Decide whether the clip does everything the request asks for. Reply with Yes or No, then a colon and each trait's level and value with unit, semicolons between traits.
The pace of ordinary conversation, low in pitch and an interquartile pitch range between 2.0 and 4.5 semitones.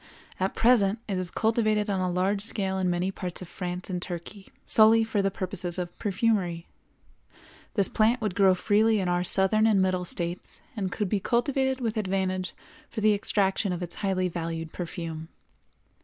No: average, 180 wpm; high, 190 Hz; average, 3.1 semitones